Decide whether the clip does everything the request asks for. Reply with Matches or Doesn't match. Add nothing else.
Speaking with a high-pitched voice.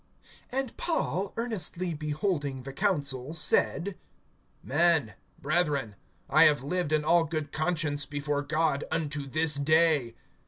Doesn't match